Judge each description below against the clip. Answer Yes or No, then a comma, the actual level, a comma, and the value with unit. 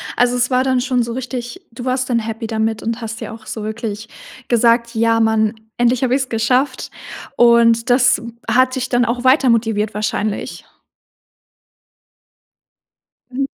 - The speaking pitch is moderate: No, high, 235 Hz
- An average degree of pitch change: No, narrow, 2.1 semitones